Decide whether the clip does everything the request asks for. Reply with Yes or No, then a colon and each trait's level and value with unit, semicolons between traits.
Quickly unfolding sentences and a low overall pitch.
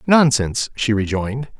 No: slow, 115 wpm; low, 120 Hz